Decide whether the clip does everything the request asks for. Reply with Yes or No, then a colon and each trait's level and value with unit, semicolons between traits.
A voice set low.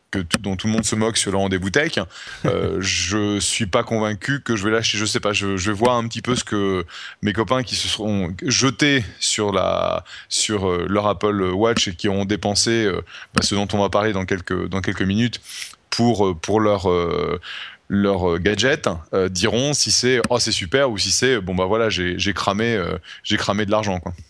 Yes: low, 105 Hz